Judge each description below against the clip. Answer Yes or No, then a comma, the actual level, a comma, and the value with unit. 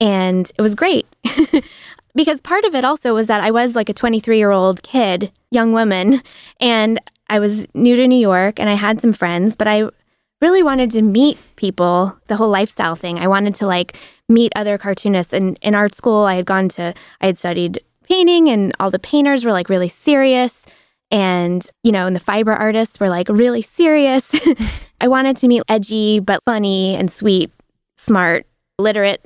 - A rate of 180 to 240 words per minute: Yes, average, 190 wpm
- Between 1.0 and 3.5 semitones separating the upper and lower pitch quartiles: No, average, 4.1 semitones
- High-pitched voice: Yes, high, 215 Hz